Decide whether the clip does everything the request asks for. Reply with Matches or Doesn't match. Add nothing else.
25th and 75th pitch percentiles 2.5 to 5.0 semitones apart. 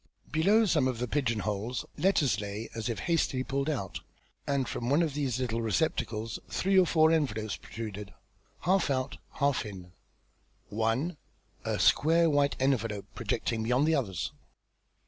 Doesn't match